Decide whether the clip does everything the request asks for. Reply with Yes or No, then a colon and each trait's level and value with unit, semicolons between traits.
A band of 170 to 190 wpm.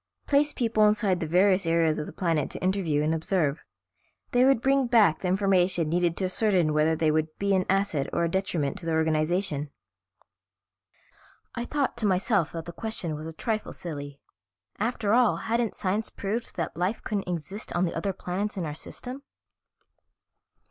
Yes: average, 175 wpm